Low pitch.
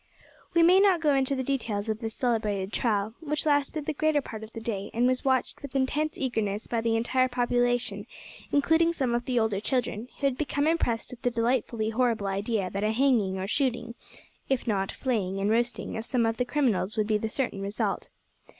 No: high, 240 Hz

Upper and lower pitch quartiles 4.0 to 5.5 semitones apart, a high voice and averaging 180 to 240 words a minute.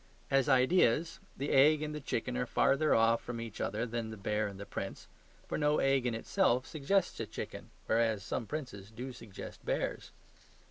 No: average, 4.4 semitones; low, 125 Hz; average, 185 wpm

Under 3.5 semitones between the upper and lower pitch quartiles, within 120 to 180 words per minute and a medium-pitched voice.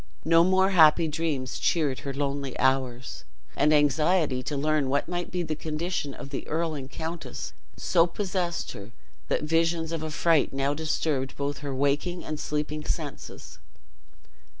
Yes: average, 2.9 semitones; average, 150 wpm; medium, 155 Hz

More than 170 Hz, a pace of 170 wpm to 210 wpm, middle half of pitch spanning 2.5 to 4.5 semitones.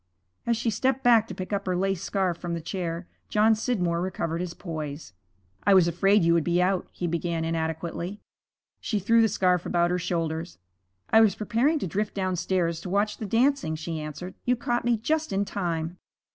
Yes: medium, 185 Hz; average, 195 wpm; average, 4.0 semitones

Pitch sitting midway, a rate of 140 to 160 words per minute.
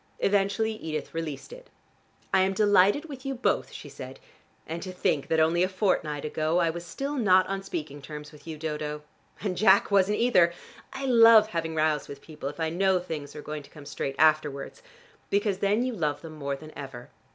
No: medium, 170 Hz; average, 200 wpm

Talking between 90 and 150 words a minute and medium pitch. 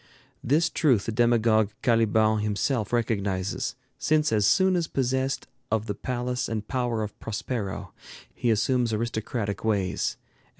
No: average, 140 wpm; low, 115 Hz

